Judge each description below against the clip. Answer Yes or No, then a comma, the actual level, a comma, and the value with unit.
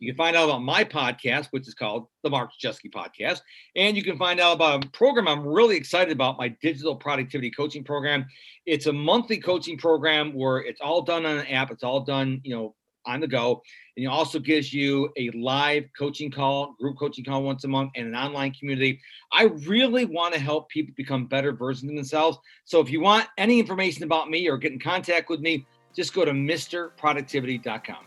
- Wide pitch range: No, average, 3.5 semitones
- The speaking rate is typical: No, fast, 210 wpm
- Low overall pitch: No, medium, 145 Hz